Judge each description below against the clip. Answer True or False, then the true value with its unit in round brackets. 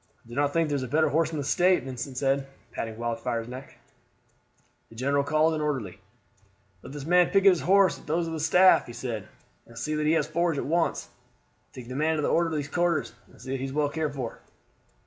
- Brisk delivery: True (230 wpm)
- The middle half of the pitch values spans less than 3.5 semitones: False (4.0 semitones)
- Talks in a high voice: False (145 Hz)